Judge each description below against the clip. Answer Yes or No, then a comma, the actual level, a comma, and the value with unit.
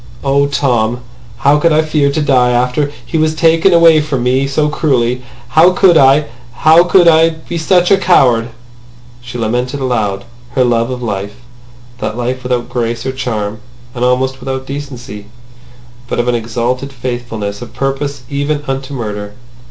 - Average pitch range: Yes, average, 3.6 semitones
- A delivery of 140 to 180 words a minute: Yes, average, 165 wpm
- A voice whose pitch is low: Yes, low, 130 Hz